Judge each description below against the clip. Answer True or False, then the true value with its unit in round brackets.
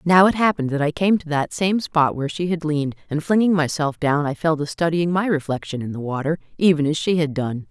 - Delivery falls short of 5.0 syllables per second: False (5.9 syllables/s)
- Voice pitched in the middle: True (160 Hz)